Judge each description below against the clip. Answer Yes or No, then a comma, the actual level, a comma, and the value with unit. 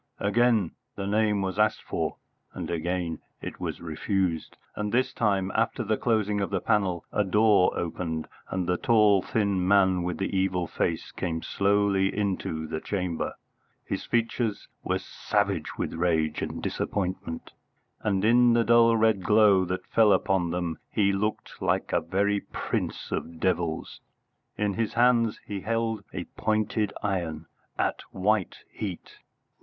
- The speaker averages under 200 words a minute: Yes, average, 150 wpm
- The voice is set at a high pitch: No, low, 100 Hz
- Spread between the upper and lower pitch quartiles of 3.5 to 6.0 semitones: No, average, 3.1 semitones